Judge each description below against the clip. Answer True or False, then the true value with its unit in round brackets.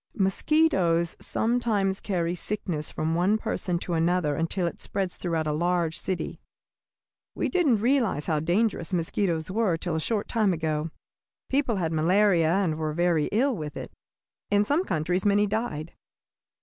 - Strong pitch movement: False (4.3 semitones)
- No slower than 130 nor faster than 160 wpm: True (150 wpm)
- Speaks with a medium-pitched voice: True (180 Hz)